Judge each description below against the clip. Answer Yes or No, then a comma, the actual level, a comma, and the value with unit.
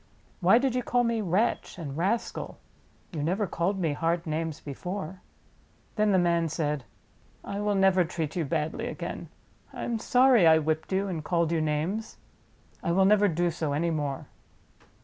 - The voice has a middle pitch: Yes, medium, 175 Hz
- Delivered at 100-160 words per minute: No, average, 170 wpm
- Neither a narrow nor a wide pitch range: Yes, average, 4.2 semitones